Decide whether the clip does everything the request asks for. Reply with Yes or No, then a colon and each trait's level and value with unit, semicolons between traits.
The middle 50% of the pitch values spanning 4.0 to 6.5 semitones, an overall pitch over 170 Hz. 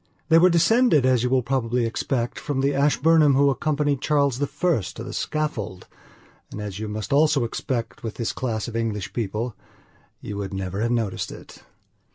No: average, 4.7 semitones; low, 125 Hz